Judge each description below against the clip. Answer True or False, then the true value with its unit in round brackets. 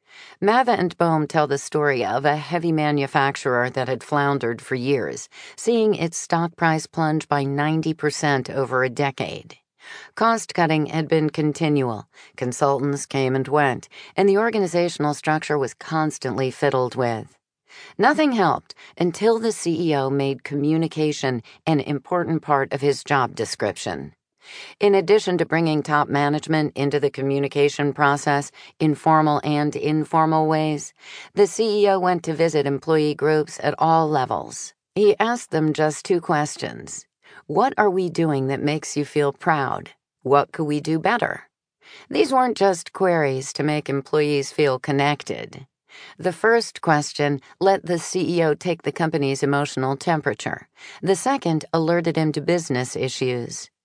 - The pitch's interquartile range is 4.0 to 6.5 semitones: False (3.1 semitones)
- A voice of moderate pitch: True (150 Hz)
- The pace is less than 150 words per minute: True (140 wpm)